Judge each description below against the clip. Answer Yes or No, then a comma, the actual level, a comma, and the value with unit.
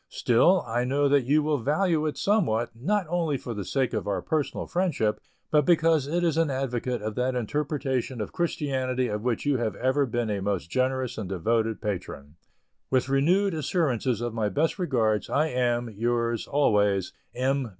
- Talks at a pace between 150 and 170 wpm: No, average, 180 wpm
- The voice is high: No, low, 130 Hz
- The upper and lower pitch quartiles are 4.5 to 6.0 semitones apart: Yes, average, 4.9 semitones